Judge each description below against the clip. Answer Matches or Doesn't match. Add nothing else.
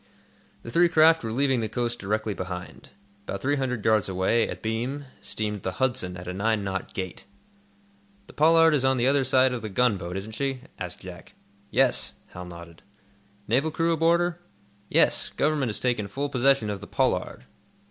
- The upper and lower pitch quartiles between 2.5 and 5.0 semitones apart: Doesn't match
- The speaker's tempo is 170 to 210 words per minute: Matches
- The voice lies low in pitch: Matches